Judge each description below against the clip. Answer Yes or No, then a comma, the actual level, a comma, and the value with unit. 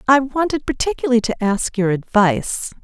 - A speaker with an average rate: Yes, average, 150 wpm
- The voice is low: No, high, 240 Hz